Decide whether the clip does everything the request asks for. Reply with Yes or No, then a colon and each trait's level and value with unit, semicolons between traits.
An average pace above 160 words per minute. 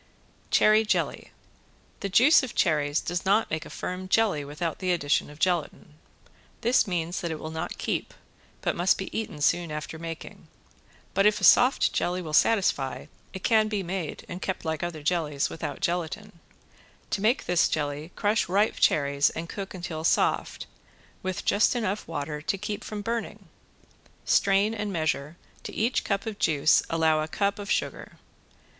Yes: average, 170 wpm